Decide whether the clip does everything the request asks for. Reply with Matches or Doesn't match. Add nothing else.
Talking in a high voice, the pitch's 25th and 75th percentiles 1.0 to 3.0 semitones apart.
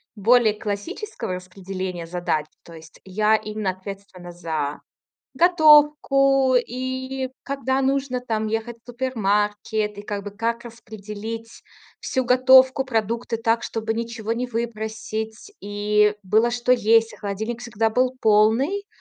Doesn't match